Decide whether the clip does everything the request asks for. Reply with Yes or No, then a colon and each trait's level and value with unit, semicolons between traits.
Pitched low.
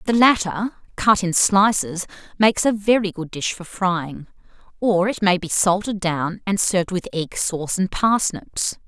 No: high, 190 Hz